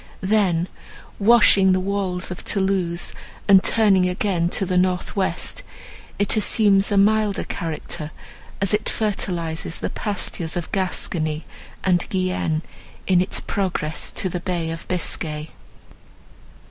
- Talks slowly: Yes, slow, 125 wpm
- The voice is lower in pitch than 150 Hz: No, medium, 185 Hz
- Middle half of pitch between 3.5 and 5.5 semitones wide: No, narrow, 2.6 semitones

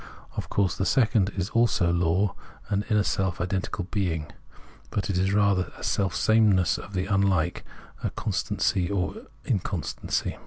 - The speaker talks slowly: No, average, 150 wpm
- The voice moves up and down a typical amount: No, narrow, 2.0 semitones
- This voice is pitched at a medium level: No, very low, 95 Hz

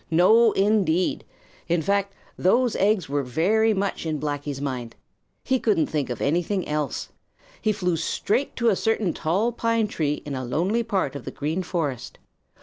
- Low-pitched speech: No, medium, 180 Hz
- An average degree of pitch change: No, wide, 6.2 semitones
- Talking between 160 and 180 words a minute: Yes, average, 165 wpm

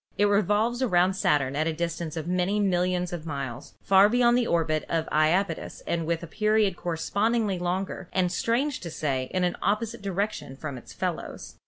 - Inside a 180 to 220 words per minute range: Yes, average, 185 wpm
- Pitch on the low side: No, medium, 180 Hz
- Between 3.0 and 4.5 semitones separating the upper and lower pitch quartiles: Yes, average, 4.1 semitones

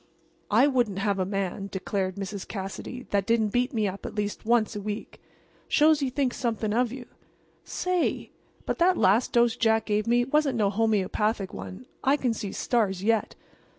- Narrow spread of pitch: No, average, 3.6 semitones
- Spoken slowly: No, average, 180 wpm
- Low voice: No, high, 220 Hz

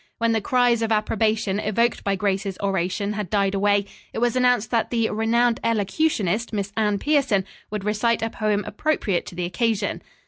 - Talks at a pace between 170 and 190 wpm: Yes, average, 175 wpm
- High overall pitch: Yes, high, 215 Hz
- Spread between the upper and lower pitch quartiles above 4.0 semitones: No, narrow, 2.6 semitones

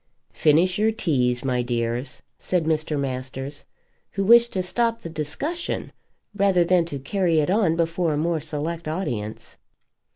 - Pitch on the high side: No, medium, 160 Hz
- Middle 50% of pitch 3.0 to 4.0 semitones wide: No, average, 4.9 semitones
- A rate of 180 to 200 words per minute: No, average, 150 wpm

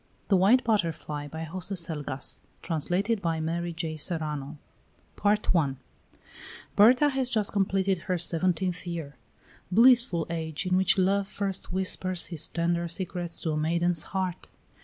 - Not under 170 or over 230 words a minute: No, average, 140 wpm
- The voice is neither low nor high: Yes, medium, 175 Hz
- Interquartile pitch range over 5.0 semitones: No, average, 3.1 semitones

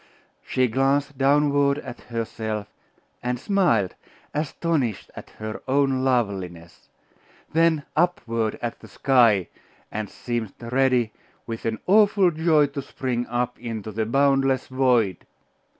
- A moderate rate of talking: No, slow, 120 wpm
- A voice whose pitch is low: Yes, low, 125 Hz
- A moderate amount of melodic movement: Yes, average, 4.0 semitones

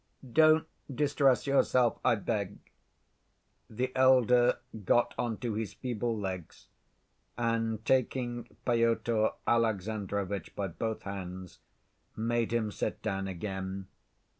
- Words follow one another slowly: Yes, slow, 105 wpm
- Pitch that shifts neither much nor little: Yes, average, 3.3 semitones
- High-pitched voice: No, low, 115 Hz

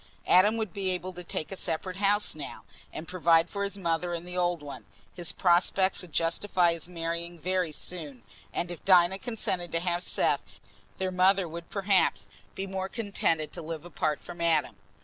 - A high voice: No, medium, 175 Hz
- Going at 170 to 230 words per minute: Yes, average, 185 wpm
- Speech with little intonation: Yes, narrow, 2.2 semitones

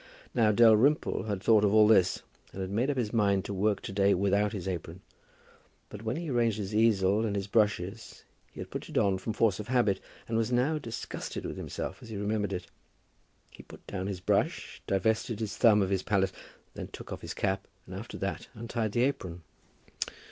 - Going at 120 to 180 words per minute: No, fast, 205 wpm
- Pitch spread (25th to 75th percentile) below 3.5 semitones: Yes, average, 2.7 semitones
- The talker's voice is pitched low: Yes, low, 105 Hz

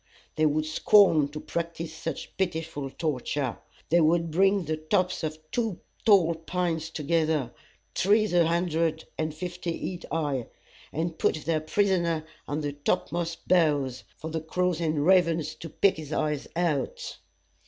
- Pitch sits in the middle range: Yes, medium, 160 Hz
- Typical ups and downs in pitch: No, narrow, 2.1 semitones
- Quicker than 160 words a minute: No, average, 145 wpm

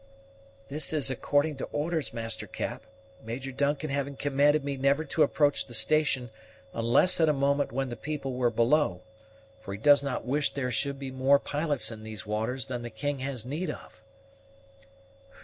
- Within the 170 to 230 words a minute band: Yes, average, 175 wpm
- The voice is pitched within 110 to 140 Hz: Yes, low, 135 Hz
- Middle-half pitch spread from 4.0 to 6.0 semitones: No, average, 3.2 semitones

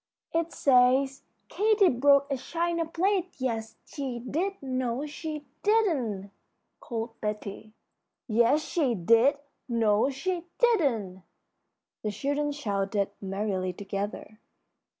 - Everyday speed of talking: No, slow, 110 wpm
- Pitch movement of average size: No, wide, 6.5 semitones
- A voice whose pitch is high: Yes, very high, 260 Hz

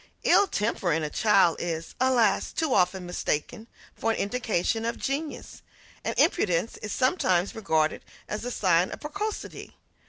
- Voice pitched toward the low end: No, high, 210 Hz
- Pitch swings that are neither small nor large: No, wide, 6.1 semitones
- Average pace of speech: Yes, average, 150 wpm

